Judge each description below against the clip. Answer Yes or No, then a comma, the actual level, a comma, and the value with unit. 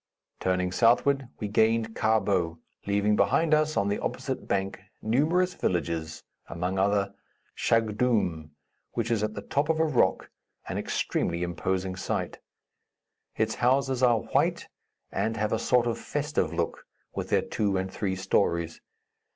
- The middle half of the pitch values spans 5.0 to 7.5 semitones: No, average, 4.5 semitones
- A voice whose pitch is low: Yes, low, 105 Hz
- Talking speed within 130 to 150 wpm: Yes, average, 145 wpm